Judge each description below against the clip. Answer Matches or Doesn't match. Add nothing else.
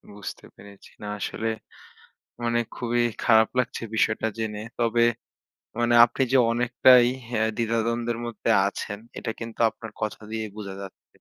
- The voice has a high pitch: Doesn't match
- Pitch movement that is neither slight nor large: Doesn't match